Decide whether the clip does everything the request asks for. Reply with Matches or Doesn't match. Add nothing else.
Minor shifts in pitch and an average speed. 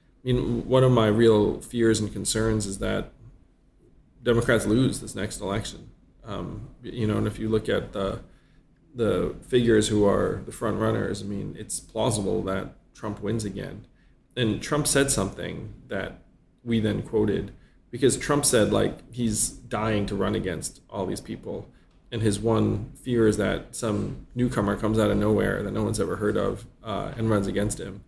Matches